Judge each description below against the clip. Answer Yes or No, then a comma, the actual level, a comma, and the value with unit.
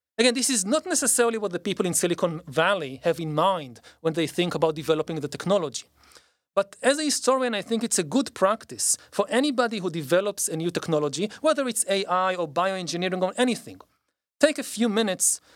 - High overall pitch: Yes, high, 195 Hz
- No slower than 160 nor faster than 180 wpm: No, average, 190 wpm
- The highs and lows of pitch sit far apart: Yes, wide, 6.1 semitones